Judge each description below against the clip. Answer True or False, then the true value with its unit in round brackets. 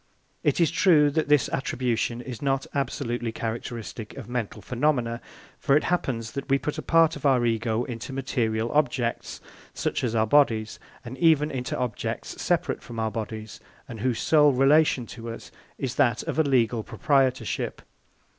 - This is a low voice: True (125 Hz)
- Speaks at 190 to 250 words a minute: False (165 wpm)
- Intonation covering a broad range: False (3.6 semitones)